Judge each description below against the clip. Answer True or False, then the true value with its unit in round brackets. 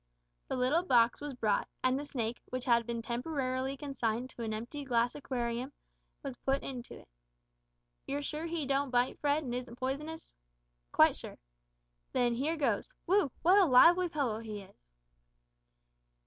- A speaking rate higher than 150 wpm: True (160 wpm)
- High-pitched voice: True (260 Hz)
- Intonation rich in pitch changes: False (3.5 semitones)